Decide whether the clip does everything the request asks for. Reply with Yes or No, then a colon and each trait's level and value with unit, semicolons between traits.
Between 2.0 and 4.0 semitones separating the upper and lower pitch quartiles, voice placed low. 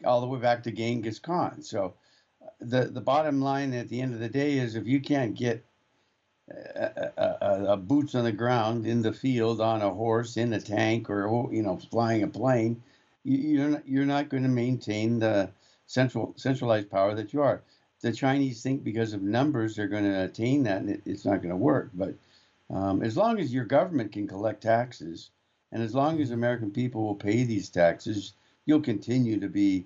Yes: average, 3.7 semitones; low, 120 Hz